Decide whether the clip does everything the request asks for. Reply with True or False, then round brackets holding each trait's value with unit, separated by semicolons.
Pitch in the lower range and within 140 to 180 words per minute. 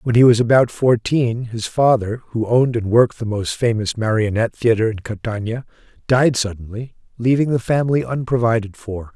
True (115 Hz; 165 wpm)